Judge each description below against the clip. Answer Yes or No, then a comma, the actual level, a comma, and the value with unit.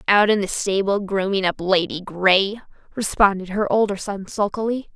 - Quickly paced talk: No, average, 155 wpm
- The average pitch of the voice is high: Yes, high, 195 Hz